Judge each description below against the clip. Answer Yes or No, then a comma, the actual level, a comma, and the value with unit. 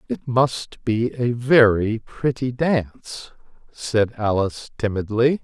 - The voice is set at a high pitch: No, low, 115 Hz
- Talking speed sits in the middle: No, slow, 110 wpm